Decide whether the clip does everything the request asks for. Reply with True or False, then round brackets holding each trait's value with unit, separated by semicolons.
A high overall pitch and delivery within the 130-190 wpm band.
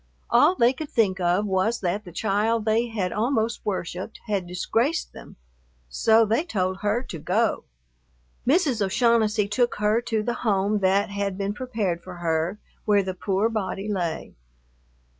True (210 Hz; 160 wpm)